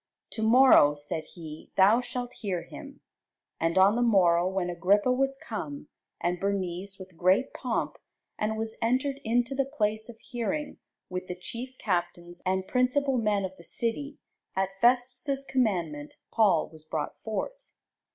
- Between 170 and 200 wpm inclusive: No, average, 150 wpm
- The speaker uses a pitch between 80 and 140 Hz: No, high, 210 Hz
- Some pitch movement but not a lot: No, wide, 5.7 semitones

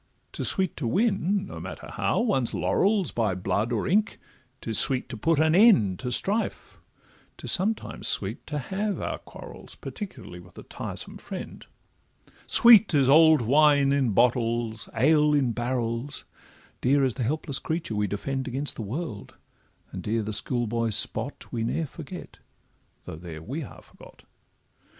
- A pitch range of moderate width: No, wide, 6.1 semitones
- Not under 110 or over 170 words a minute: Yes, average, 155 wpm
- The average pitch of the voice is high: No, low, 130 Hz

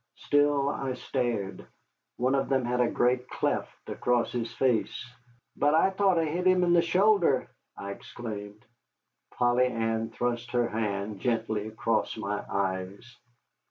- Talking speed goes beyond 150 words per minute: No, average, 145 wpm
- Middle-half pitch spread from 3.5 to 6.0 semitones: Yes, average, 4.2 semitones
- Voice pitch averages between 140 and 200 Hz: No, low, 120 Hz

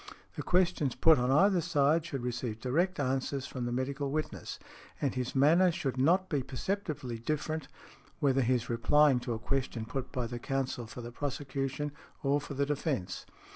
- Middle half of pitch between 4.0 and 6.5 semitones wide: No, average, 3.2 semitones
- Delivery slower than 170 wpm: No, average, 175 wpm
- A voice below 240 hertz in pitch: Yes, low, 135 Hz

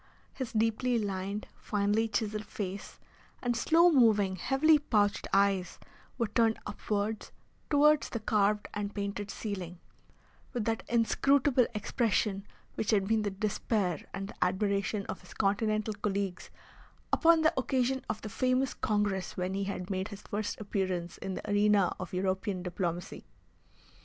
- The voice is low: No, high, 210 Hz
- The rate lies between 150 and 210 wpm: No, average, 140 wpm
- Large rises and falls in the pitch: No, average, 2.7 semitones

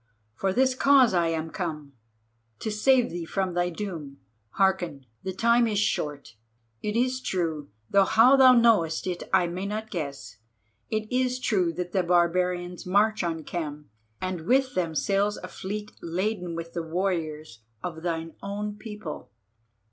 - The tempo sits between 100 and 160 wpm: Yes, average, 150 wpm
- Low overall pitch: No, medium, 180 Hz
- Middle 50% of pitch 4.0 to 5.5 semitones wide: Yes, average, 4.4 semitones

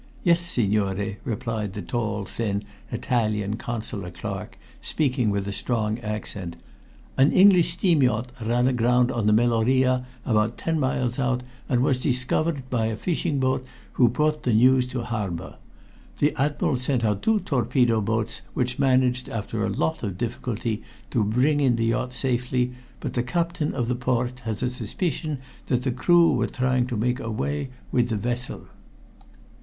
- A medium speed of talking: Yes, average, 160 wpm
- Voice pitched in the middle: No, low, 125 Hz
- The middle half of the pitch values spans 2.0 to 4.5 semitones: Yes, average, 2.9 semitones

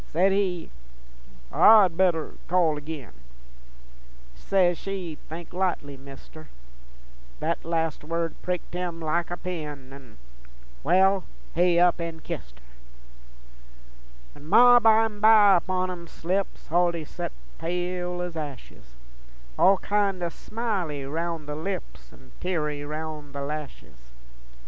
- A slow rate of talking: Yes, slow, 120 wpm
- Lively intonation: No, average, 3.5 semitones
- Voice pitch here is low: No, medium, 170 Hz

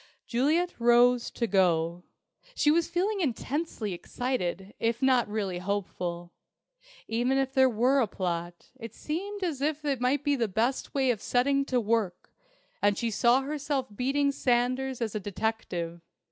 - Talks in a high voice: Yes, high, 245 Hz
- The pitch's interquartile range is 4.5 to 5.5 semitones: Yes, average, 5.1 semitones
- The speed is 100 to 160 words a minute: Yes, average, 155 wpm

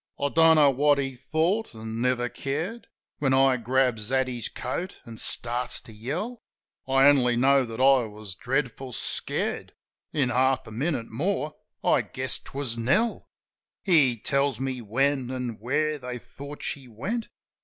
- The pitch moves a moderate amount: Yes, average, 3.0 semitones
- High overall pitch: No, low, 130 Hz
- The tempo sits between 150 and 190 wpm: Yes, average, 155 wpm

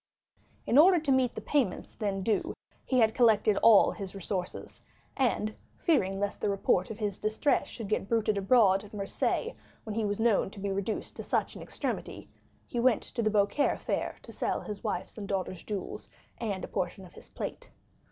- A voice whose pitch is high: Yes, high, 210 Hz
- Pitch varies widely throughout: No, average, 2.9 semitones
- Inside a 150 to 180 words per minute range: No, average, 190 wpm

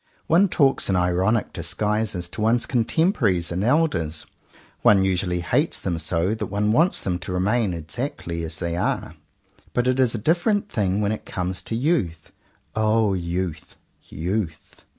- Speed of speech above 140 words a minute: Yes, average, 155 wpm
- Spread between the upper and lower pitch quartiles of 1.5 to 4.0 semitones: No, average, 5.2 semitones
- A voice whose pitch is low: Yes, low, 100 Hz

